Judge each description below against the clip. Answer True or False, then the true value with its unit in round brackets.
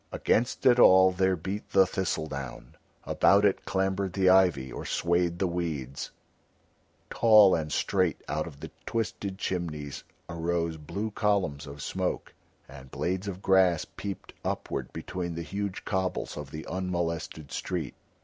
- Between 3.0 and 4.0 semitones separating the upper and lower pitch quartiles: True (3.5 semitones)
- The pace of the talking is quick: False (145 wpm)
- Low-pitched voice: True (90 Hz)